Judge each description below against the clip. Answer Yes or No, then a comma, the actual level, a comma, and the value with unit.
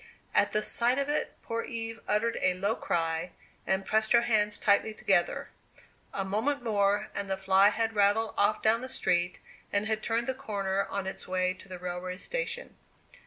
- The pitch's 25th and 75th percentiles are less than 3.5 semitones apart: Yes, average, 3.0 semitones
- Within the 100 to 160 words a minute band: No, average, 185 wpm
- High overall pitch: Yes, high, 205 Hz